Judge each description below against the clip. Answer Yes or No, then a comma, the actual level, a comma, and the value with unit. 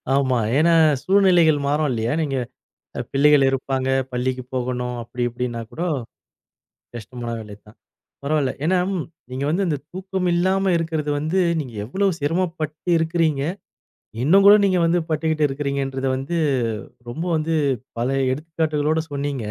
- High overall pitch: No, medium, 145 Hz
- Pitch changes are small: No, average, 4.3 semitones